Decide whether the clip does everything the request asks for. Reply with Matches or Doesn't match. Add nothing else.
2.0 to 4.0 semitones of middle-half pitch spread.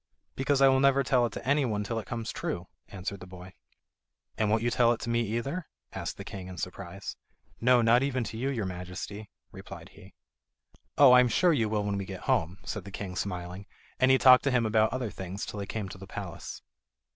Doesn't match